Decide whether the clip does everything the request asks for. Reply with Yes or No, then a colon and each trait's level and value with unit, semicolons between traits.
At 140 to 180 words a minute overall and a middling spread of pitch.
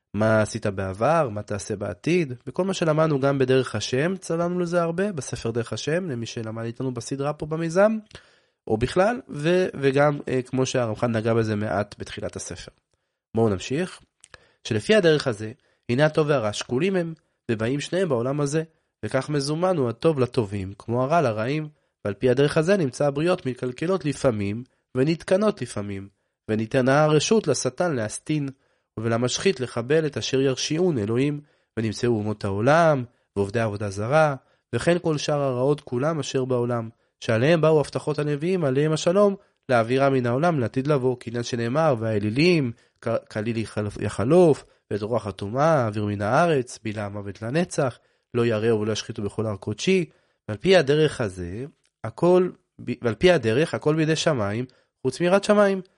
No: average, 145 wpm; wide, 5.9 semitones